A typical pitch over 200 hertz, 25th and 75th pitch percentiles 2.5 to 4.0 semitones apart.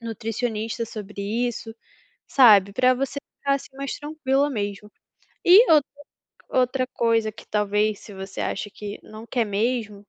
Yes: high, 225 Hz; average, 3.6 semitones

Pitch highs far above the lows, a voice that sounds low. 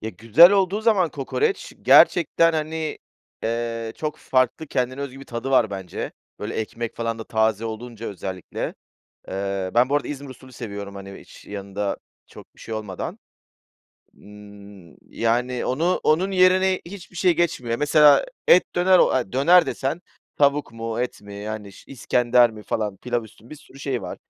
Yes: wide, 6.0 semitones; low, 120 Hz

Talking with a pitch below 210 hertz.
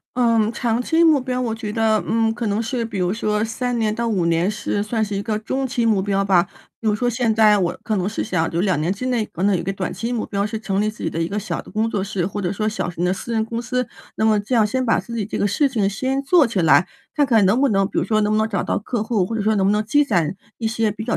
No: high, 215 Hz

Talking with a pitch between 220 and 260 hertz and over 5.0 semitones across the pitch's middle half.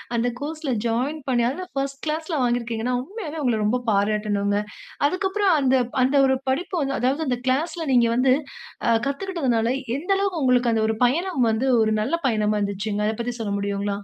Yes: very high, 255 Hz; wide, 5.6 semitones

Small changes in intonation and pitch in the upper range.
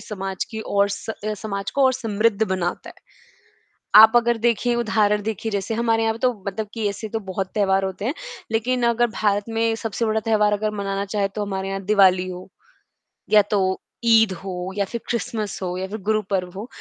Yes: narrow, 2.3 semitones; high, 210 Hz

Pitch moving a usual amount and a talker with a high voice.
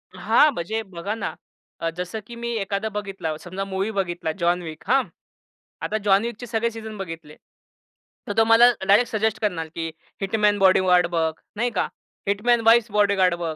Yes: average, 3.9 semitones; high, 200 Hz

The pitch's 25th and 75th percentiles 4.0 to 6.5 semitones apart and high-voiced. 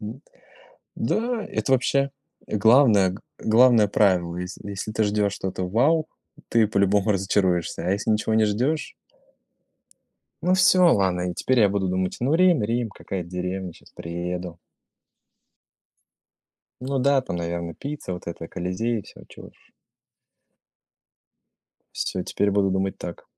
No: average, 5.2 semitones; low, 100 Hz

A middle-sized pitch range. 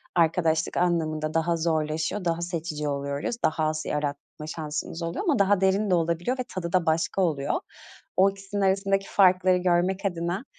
Yes: average, 3.3 semitones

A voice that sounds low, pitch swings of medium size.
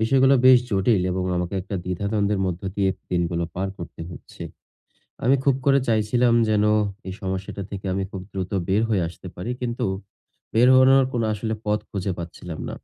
Yes: low, 100 Hz; average, 4.1 semitones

